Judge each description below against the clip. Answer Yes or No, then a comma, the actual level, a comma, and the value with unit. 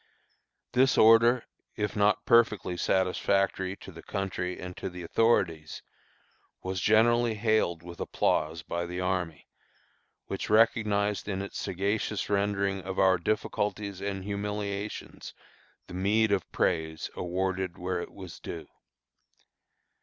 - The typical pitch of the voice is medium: No, very low, 95 Hz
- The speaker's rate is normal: No, slow, 125 wpm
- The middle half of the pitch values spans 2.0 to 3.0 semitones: Yes, narrow, 2.6 semitones